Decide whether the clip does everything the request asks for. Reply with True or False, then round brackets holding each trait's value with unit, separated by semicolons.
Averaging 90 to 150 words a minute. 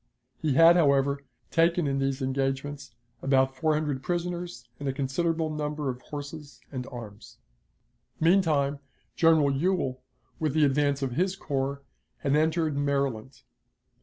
True (135 wpm)